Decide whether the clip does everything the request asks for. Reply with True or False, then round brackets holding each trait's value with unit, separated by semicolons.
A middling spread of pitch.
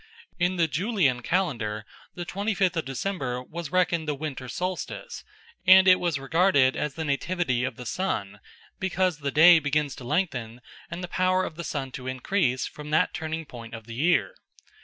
False (5.8 semitones)